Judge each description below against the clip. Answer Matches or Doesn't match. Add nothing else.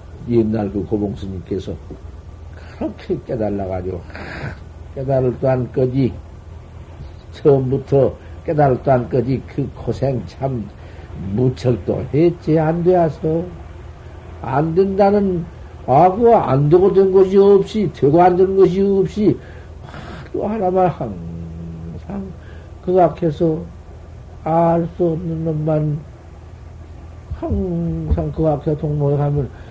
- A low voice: Matches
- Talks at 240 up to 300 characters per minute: Doesn't match